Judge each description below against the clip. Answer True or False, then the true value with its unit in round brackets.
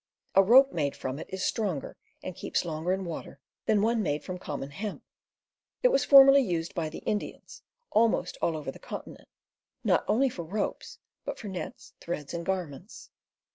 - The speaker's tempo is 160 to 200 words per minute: True (175 wpm)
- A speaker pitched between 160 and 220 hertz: True (185 Hz)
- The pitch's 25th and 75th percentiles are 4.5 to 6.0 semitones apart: True (5.3 semitones)